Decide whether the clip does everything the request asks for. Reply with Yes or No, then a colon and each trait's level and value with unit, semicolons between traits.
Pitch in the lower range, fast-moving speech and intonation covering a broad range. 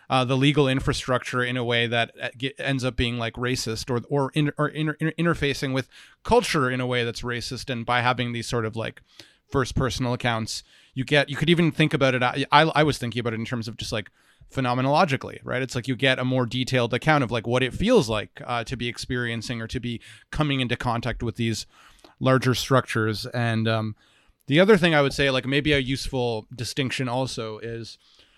No: low, 125 Hz; fast, 215 wpm; narrow, 2.6 semitones